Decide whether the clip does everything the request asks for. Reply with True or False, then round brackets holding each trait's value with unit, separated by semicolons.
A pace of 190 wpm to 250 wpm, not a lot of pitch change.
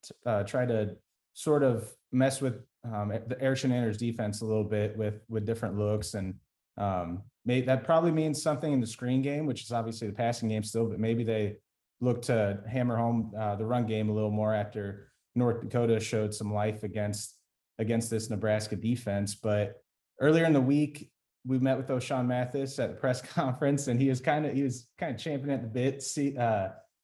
False (200 wpm; 3.6 semitones)